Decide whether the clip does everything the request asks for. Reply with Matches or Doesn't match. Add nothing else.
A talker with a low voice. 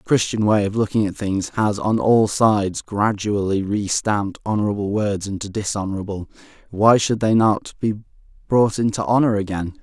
Matches